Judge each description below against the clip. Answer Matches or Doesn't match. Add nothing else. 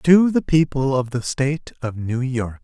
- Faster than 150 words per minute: Matches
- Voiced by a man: Matches